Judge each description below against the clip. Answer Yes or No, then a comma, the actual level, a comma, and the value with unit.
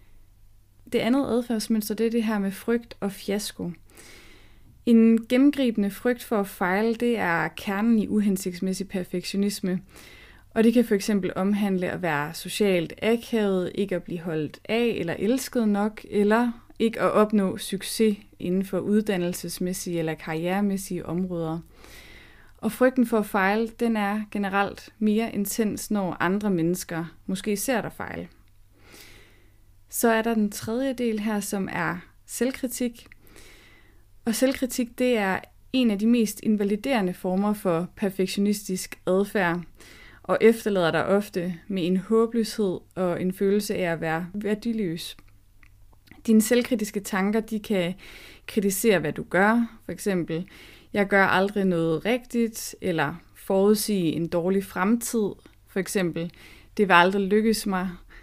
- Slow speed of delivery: Yes, slow, 135 wpm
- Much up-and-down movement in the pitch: No, average, 4.3 semitones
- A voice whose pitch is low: No, high, 200 Hz